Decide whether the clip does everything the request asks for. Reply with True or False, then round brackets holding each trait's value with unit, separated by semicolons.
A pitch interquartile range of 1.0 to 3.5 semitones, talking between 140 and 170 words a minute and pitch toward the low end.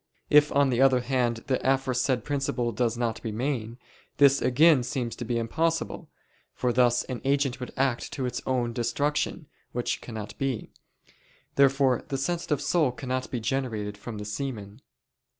True (2.5 semitones; 155 wpm; 125 Hz)